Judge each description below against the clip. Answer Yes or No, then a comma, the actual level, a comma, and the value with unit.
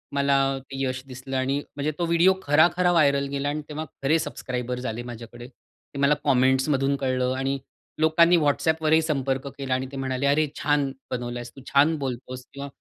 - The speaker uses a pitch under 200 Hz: Yes, medium, 140 Hz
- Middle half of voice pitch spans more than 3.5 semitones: No, average, 2.8 semitones